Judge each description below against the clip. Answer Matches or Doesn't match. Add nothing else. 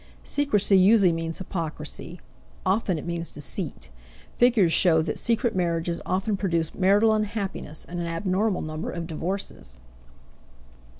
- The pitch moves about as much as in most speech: Matches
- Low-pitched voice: Doesn't match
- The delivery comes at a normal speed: Doesn't match